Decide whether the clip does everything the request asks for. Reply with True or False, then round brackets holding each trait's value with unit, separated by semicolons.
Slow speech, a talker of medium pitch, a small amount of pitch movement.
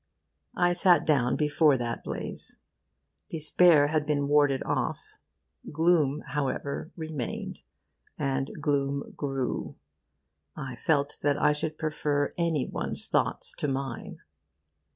True (110 wpm; 145 Hz; 2.1 semitones)